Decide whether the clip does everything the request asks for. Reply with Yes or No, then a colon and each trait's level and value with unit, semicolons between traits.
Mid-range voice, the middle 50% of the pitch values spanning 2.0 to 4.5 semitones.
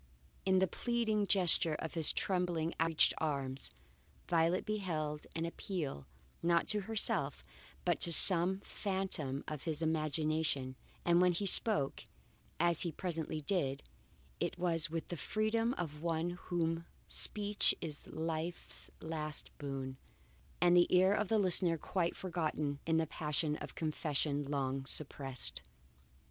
Yes: medium, 165 Hz; average, 3.2 semitones